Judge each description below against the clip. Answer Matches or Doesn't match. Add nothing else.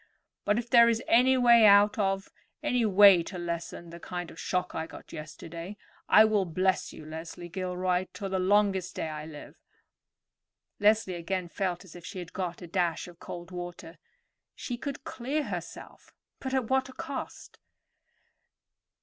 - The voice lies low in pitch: Doesn't match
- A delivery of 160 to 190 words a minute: Matches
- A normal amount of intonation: Matches